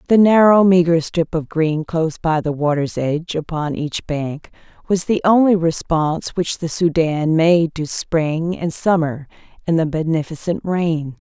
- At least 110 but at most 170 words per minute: Yes, average, 160 wpm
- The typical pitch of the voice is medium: Yes, medium, 165 Hz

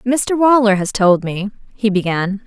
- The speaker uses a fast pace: No, average, 170 wpm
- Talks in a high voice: Yes, high, 215 Hz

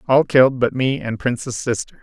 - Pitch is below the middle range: Yes, low, 125 Hz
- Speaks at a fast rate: Yes, fast, 210 wpm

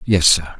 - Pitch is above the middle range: No, very low, 80 Hz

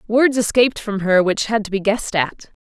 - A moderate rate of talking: No, fast, 230 wpm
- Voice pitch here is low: No, high, 210 Hz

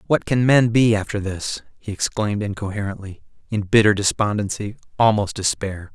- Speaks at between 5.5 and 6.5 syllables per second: No, 5.3 syllables/s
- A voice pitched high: No, low, 105 Hz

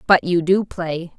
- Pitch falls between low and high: Yes, medium, 175 Hz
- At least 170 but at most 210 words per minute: Yes, average, 200 wpm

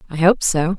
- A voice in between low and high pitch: Yes, medium, 175 Hz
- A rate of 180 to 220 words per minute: No, fast, 230 wpm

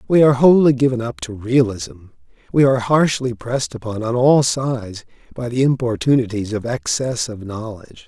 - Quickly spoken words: No, average, 165 wpm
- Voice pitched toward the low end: Yes, low, 120 Hz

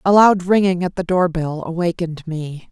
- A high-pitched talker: No, medium, 175 Hz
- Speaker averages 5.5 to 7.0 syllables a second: No, 5.1 syllables/s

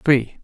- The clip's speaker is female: No, male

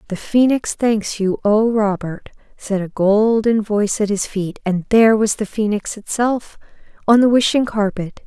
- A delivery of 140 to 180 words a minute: Yes, average, 165 wpm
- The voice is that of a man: No, female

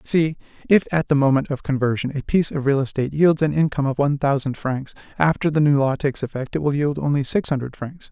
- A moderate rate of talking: No, fast, 235 wpm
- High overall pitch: No, medium, 145 Hz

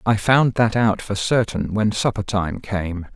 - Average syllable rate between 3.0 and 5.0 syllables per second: Yes, 4.0 syllables/s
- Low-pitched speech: Yes, low, 105 Hz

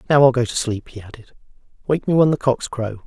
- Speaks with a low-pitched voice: Yes, low, 125 Hz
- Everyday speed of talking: No, fast, 255 wpm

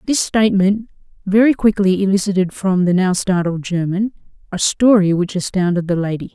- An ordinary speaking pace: Yes, average, 150 wpm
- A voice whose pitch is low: No, high, 190 Hz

